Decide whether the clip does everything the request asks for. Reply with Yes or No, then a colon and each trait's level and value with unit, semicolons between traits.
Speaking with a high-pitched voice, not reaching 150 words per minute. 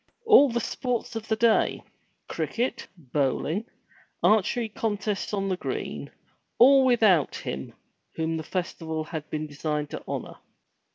Yes: high, 195 Hz; slow, 135 wpm